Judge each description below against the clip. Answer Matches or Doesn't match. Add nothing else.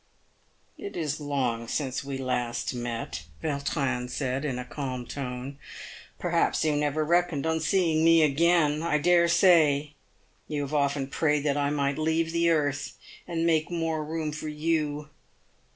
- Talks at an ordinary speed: Matches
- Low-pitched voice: Doesn't match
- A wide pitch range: Doesn't match